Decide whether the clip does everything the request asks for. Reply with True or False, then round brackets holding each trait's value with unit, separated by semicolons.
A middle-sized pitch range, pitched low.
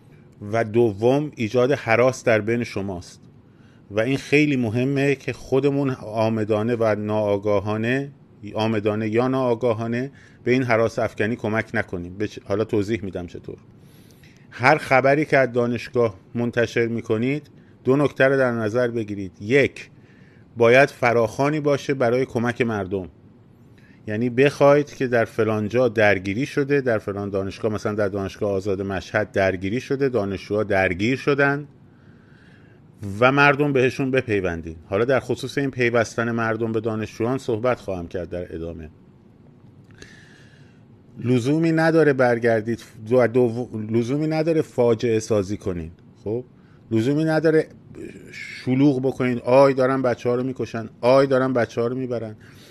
True (3.5 semitones; 120 Hz)